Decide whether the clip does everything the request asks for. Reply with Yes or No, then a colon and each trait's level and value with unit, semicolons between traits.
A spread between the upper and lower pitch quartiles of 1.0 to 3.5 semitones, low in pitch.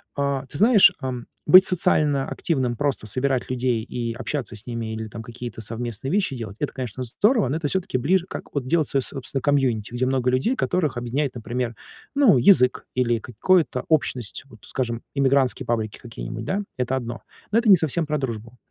No: average, 4.0 semitones; low, 130 Hz